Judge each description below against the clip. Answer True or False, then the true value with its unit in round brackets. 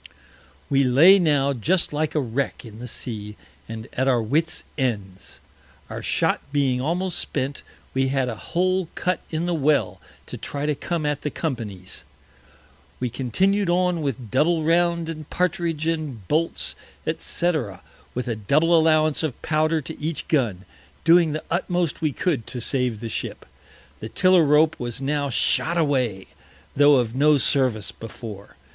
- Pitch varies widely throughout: False (4.9 semitones)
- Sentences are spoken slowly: False (160 wpm)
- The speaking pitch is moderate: True (145 Hz)